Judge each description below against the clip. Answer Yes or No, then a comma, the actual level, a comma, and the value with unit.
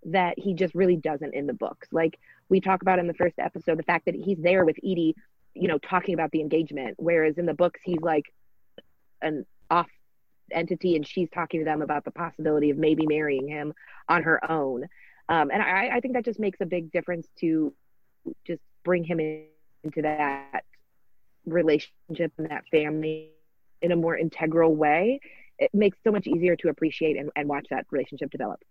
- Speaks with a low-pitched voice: No, medium, 165 Hz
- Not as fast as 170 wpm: No, average, 195 wpm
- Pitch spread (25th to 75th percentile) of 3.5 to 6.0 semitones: No, average, 2.7 semitones